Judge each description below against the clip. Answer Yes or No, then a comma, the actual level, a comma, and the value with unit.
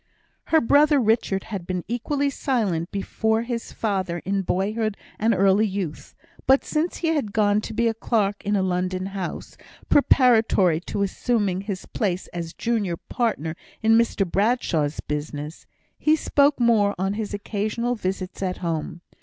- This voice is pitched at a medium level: No, high, 205 Hz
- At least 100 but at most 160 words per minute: Yes, average, 150 wpm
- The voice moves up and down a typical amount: Yes, average, 3.9 semitones